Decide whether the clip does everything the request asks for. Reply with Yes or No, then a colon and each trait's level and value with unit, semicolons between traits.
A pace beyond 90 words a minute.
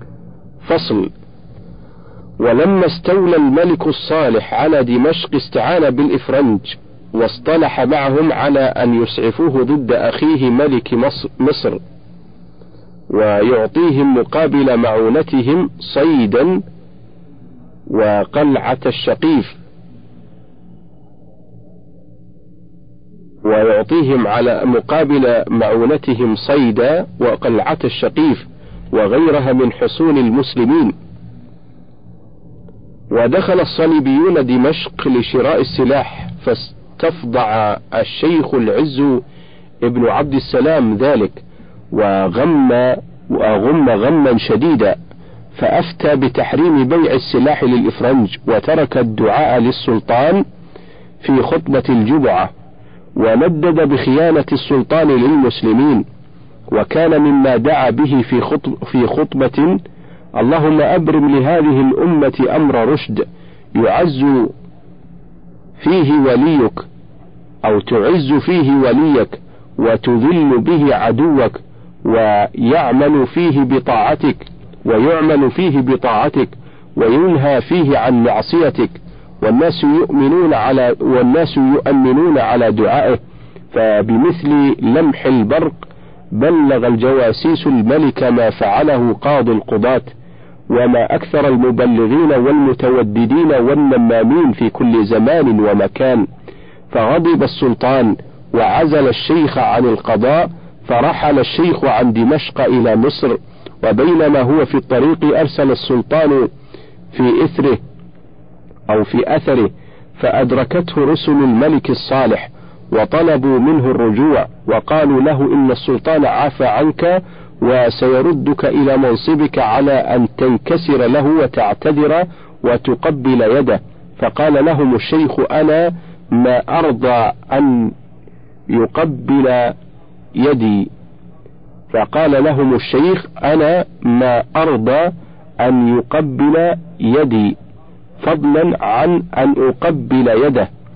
No: average, 85 wpm